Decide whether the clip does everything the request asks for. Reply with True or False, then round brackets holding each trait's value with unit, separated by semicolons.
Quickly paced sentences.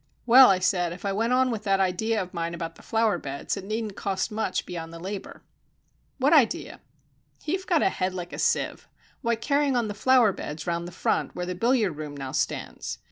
True (215 wpm)